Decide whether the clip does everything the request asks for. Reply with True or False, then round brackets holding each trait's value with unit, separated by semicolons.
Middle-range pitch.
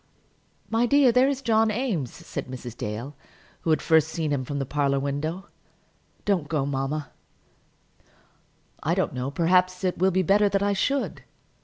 True (165 Hz)